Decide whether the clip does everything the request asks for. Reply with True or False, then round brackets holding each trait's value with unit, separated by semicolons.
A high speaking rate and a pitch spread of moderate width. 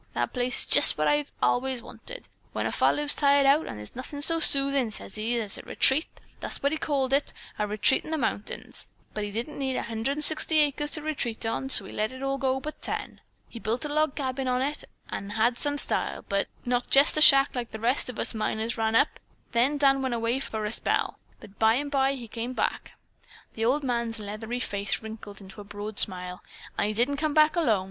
True (215 wpm; 4.2 semitones)